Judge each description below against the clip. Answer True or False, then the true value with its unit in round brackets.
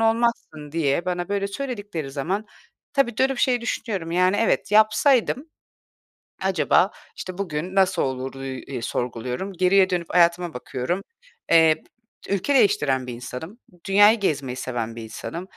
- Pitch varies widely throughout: True (7.1 semitones)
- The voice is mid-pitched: True (180 Hz)